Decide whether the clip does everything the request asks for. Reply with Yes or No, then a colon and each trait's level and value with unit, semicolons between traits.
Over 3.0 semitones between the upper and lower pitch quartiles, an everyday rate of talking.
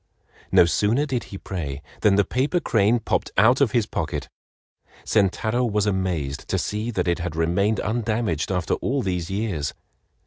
Yes: average, 4.3 semitones; average, 165 wpm